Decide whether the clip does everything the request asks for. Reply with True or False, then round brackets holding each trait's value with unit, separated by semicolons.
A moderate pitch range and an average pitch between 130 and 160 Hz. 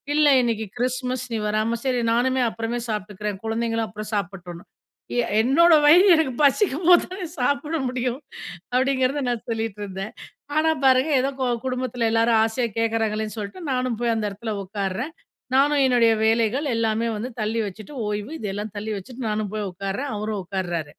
False (3.5 semitones; 230 Hz)